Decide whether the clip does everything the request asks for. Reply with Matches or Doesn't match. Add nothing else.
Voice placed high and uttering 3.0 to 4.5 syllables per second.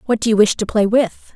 Doesn't match